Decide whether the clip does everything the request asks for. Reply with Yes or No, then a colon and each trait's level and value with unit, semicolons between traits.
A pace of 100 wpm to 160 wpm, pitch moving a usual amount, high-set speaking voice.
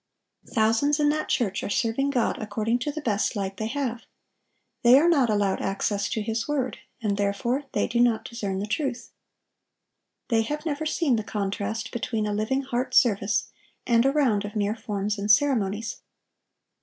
No: average, 175 wpm; average, 4.3 semitones; high, 225 Hz